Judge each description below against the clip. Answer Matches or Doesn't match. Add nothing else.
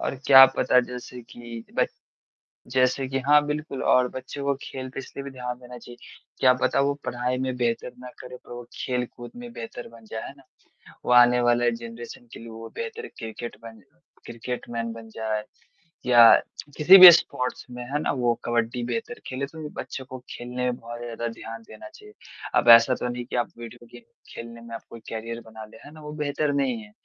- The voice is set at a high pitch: Doesn't match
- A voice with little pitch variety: Matches